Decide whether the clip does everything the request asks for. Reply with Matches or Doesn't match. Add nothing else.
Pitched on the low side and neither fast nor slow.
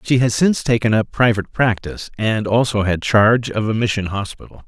Matches